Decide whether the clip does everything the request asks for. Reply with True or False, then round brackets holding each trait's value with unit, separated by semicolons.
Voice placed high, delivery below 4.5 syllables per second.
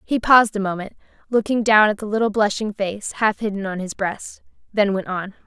False (205 Hz; 5.5 syllables/s)